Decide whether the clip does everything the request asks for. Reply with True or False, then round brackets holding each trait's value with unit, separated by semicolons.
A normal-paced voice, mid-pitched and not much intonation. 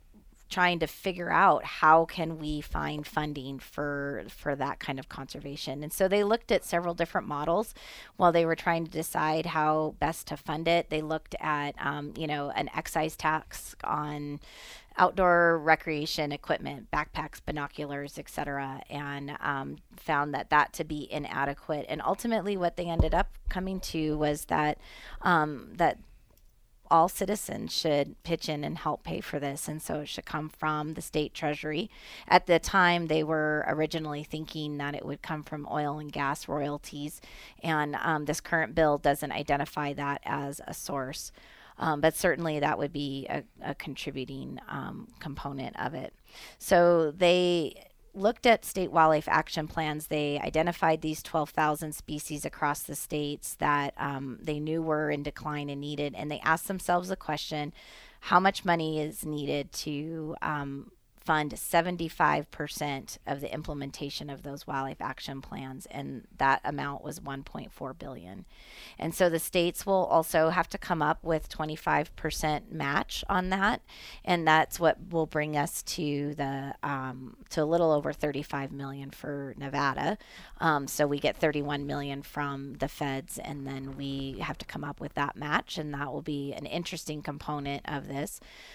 True (165 wpm; 150 Hz; 2.3 semitones)